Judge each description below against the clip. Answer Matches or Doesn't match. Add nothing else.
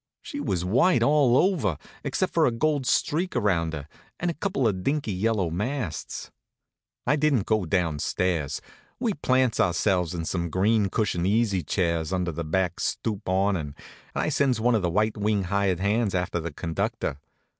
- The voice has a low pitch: Matches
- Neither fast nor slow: Matches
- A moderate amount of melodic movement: Doesn't match